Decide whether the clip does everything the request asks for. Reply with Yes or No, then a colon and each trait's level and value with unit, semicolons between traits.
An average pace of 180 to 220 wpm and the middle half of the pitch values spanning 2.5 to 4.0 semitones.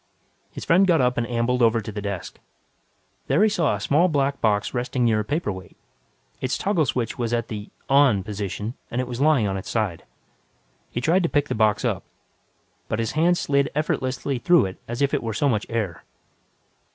No: average, 200 wpm; average, 5.0 semitones